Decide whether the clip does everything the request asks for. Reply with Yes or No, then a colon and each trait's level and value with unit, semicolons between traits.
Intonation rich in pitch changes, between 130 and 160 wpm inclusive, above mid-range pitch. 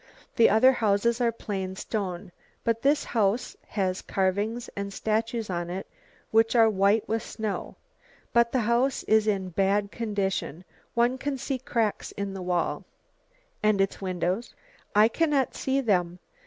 No: average, 3.3 semitones; average, 150 wpm; high, 215 Hz